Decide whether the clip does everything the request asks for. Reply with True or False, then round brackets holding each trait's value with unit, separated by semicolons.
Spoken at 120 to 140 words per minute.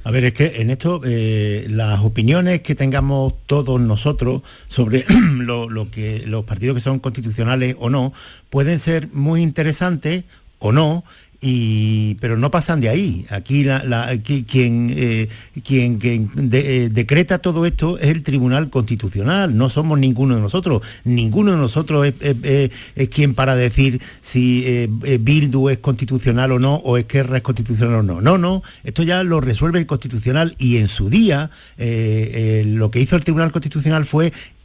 False (175 wpm)